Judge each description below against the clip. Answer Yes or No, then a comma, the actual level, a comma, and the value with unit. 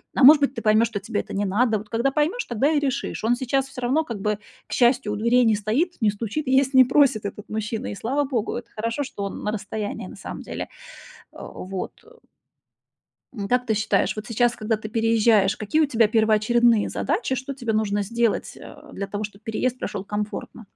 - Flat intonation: No, average, 3.4 semitones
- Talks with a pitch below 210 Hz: No, high, 225 Hz